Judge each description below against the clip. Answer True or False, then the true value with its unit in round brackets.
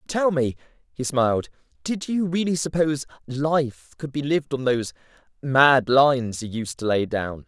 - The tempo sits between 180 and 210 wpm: False (170 wpm)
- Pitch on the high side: False (140 Hz)